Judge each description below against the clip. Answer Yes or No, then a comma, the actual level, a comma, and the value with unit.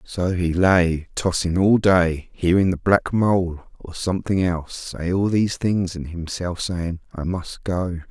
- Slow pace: No, average, 170 wpm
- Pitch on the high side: No, very low, 90 Hz